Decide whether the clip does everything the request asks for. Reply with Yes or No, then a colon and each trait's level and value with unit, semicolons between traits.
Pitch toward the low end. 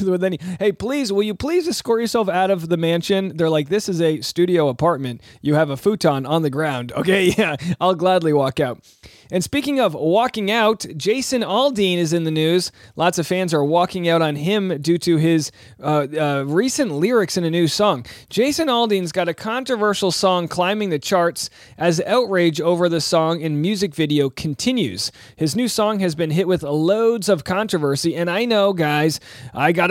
No: medium, 175 Hz